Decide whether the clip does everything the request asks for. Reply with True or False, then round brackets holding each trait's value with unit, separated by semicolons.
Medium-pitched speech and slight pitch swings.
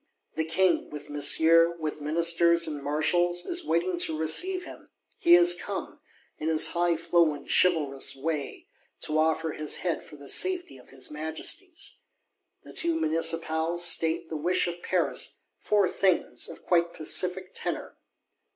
True (165 Hz; 2.2 semitones)